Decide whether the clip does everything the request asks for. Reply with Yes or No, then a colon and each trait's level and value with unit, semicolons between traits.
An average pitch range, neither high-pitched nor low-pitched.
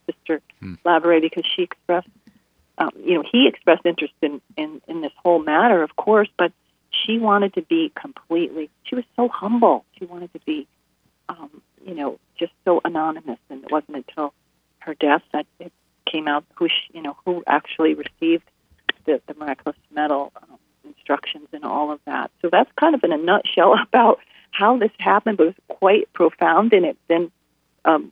No: wide, 6.2 semitones; medium, 170 Hz